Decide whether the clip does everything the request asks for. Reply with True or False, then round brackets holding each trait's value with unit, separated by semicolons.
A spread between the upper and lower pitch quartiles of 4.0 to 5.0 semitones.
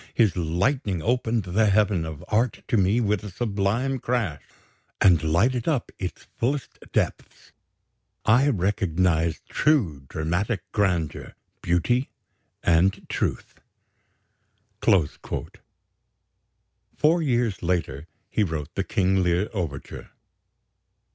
False (5.4 semitones)